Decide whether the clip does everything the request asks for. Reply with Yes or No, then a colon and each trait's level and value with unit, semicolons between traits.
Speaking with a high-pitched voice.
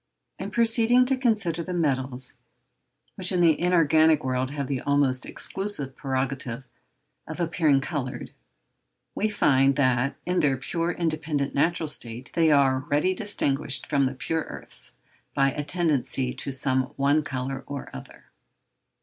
No: medium, 145 Hz